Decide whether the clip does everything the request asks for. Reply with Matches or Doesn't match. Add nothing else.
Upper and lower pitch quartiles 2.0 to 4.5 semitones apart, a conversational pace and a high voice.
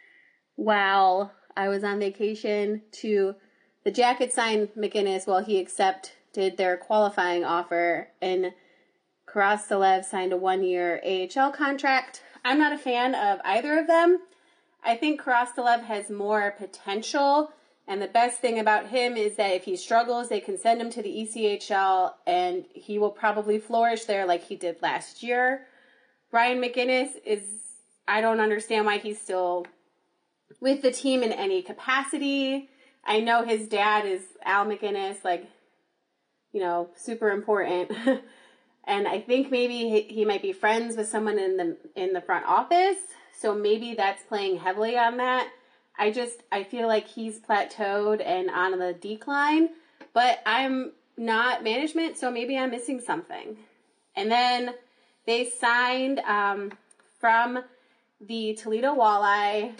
Matches